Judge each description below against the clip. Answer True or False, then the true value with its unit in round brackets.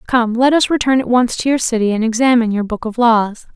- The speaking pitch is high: True (235 Hz)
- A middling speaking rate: False (255 wpm)